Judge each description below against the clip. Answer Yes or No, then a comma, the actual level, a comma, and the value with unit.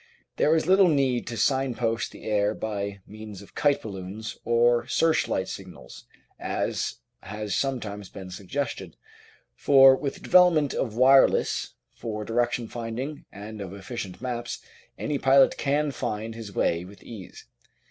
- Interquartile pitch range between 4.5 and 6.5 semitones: Yes, average, 4.8 semitones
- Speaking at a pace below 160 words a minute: Yes, average, 140 wpm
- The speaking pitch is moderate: No, low, 115 Hz